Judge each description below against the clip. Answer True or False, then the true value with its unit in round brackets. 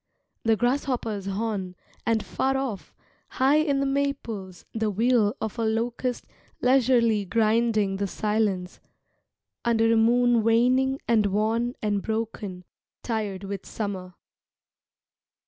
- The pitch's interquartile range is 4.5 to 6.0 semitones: False (3.1 semitones)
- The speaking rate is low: True (115 wpm)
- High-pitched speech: True (225 Hz)